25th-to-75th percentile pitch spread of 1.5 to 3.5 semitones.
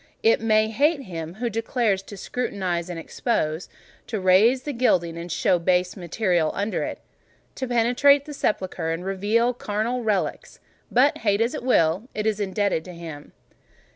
No: average, 5.0 semitones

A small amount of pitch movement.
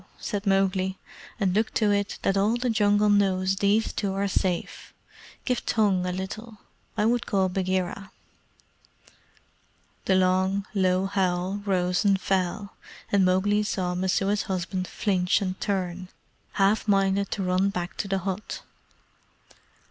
Yes: narrow, 1.7 semitones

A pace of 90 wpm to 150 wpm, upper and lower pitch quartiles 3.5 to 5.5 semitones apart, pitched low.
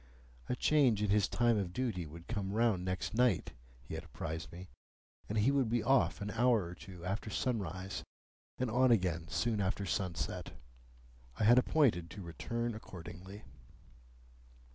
No: average, 160 wpm; average, 4.6 semitones; low, 105 Hz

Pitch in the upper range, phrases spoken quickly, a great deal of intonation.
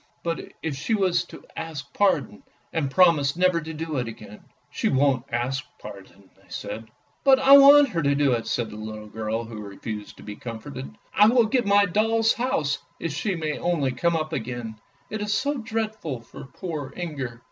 No: medium, 150 Hz; fast, 210 wpm; wide, 8.7 semitones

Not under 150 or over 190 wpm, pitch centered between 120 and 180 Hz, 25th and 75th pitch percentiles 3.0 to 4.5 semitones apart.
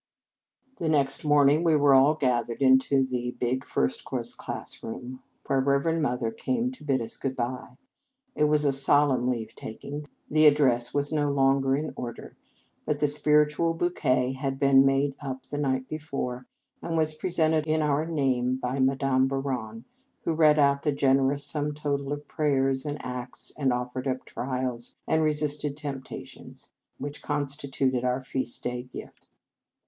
No: average, 165 wpm; medium, 140 Hz; narrow, 2.4 semitones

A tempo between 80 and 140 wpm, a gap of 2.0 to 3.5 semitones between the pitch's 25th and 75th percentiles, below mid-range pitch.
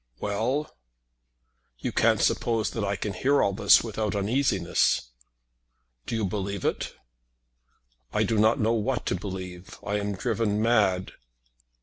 Yes: slow, 135 wpm; average, 2.7 semitones; low, 105 Hz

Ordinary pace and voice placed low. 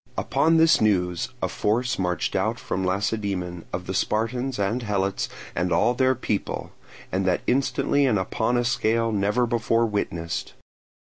Yes: average, 150 wpm; low, 110 Hz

